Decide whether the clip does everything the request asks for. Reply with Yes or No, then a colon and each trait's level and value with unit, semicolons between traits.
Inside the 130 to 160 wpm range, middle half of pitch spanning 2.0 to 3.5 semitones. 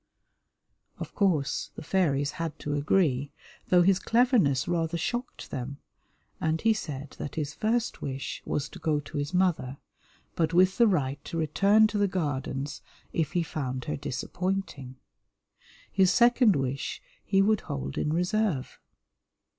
No: average, 145 wpm; wide, 5.5 semitones